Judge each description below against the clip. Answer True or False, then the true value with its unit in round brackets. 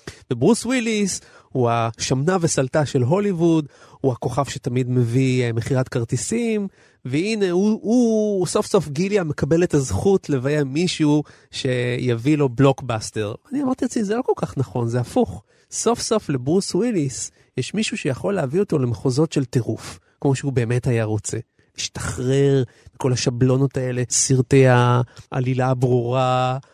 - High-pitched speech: False (135 Hz)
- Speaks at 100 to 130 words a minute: False (140 wpm)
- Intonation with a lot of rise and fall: True (6.1 semitones)